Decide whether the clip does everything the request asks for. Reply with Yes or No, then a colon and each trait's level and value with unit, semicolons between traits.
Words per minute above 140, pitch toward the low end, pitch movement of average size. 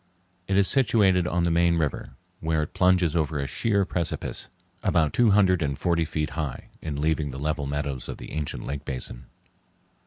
Yes: average, 185 wpm; very low, 80 Hz; average, 3.9 semitones